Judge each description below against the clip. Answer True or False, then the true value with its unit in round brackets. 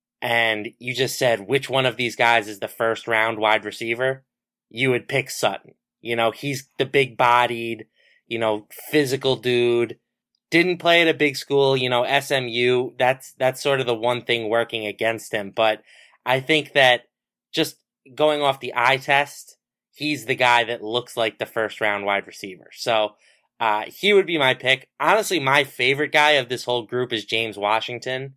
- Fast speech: False (185 wpm)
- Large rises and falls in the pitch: False (2.9 semitones)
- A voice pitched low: True (125 Hz)